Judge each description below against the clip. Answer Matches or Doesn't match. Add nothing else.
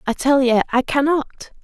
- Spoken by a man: Doesn't match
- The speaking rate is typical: Matches